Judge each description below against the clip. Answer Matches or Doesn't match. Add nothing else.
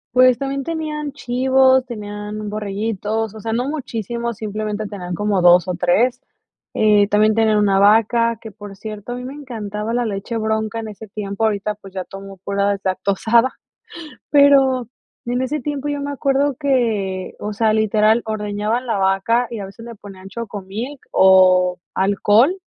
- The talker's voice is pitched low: Doesn't match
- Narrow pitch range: Doesn't match